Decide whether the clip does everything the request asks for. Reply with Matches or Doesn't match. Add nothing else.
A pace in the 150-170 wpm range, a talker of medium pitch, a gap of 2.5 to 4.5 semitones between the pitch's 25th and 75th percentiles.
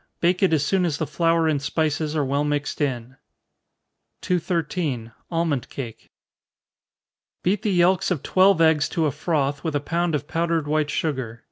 Matches